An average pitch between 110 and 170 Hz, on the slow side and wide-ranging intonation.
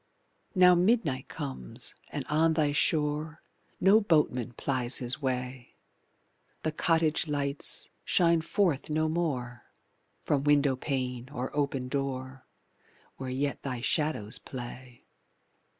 No: medium, 140 Hz; slow, 115 wpm; average, 3.6 semitones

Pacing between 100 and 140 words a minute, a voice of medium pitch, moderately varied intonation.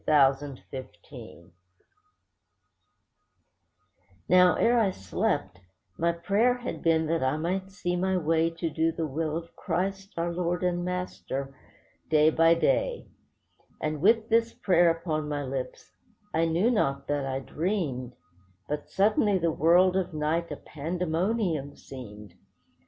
Yes: slow, 135 wpm; medium, 165 Hz; average, 3.7 semitones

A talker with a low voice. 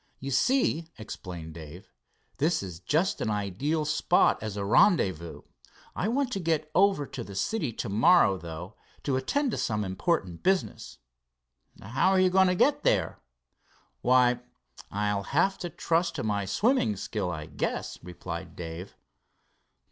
Yes: low, 125 Hz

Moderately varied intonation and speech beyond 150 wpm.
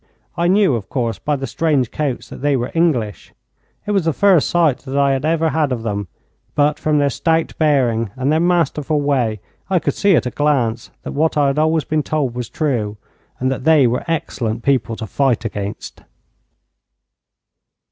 Yes: average, 4.5 semitones; average, 190 wpm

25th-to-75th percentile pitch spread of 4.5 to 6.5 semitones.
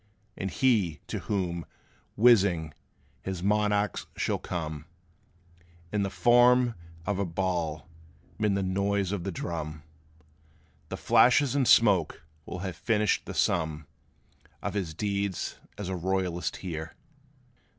No: average, 3.6 semitones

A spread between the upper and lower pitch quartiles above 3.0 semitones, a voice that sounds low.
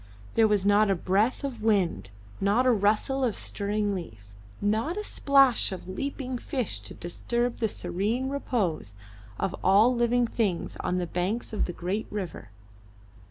No: average, 4.6 semitones; high, 210 Hz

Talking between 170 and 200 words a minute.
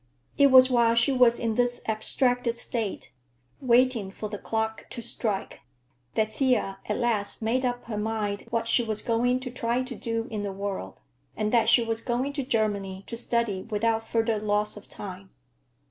Yes: average, 180 wpm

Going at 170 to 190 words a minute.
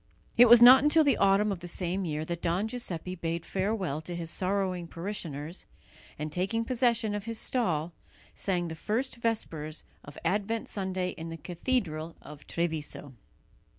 No: average, 160 wpm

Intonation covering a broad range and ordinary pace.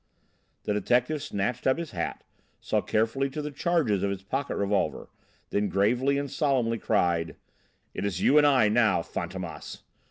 Yes: wide, 5.7 semitones; average, 160 wpm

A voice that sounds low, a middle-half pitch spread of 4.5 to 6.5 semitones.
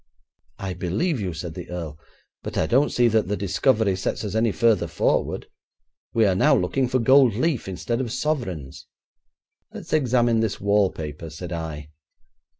Yes: low, 105 Hz; wide, 5.5 semitones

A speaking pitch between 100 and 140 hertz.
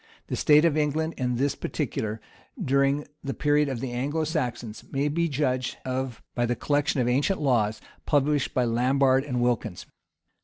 Yes: low, 135 Hz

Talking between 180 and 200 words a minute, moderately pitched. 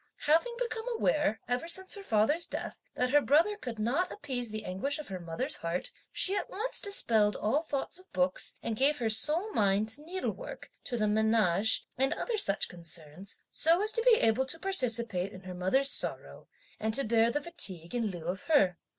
No: average, 195 wpm; high, 240 Hz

